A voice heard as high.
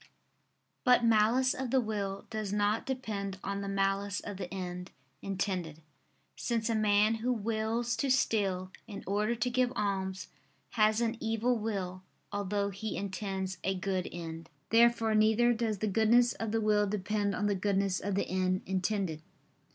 Yes: high, 205 Hz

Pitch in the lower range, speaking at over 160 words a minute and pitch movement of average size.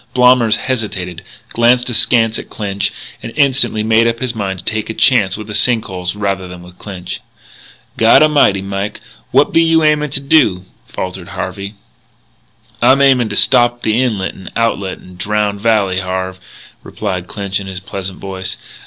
Yes: low, 105 Hz; average, 170 wpm; average, 4.2 semitones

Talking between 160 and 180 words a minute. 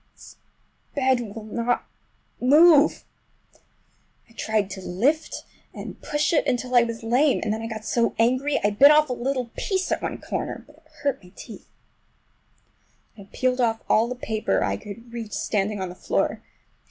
Yes: average, 175 wpm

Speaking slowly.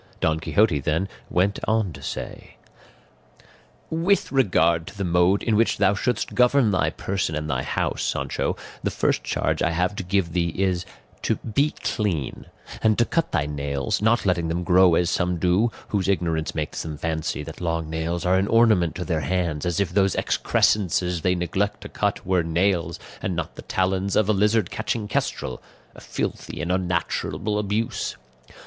No: average, 180 wpm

